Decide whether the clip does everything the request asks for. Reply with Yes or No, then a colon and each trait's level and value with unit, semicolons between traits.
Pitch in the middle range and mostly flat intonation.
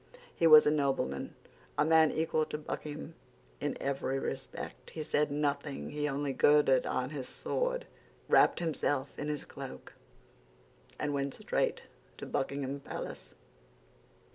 Yes: medium, 145 Hz; narrow, 1.7 semitones